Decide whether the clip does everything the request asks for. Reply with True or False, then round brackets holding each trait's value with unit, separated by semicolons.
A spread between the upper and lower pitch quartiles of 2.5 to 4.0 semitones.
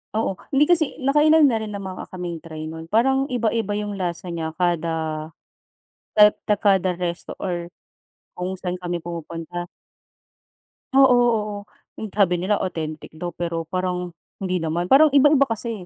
False (4.7 semitones)